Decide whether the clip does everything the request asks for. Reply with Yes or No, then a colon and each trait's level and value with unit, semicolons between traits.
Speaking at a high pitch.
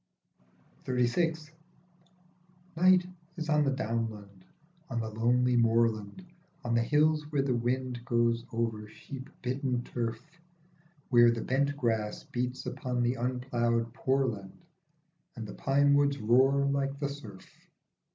No: low, 125 Hz